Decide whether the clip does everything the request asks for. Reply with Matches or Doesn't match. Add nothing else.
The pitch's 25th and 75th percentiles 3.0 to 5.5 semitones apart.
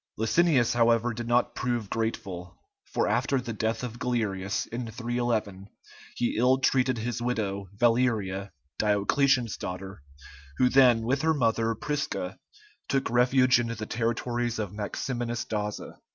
Doesn't match